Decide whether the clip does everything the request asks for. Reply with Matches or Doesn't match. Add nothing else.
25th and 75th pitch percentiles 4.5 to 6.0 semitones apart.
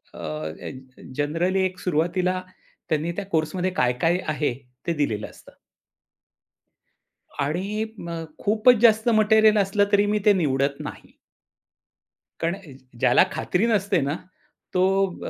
Matches